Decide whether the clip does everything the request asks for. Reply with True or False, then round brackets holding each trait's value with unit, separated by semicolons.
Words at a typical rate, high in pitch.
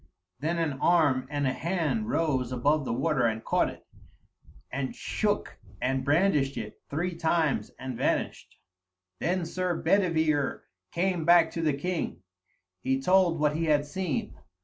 False (150 wpm; 155 Hz)